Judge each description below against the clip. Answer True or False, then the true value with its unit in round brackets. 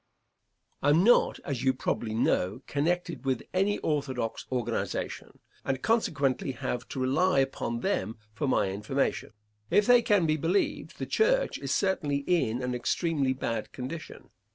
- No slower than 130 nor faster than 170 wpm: True (150 wpm)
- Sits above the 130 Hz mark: True (140 Hz)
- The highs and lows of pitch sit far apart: True (5.9 semitones)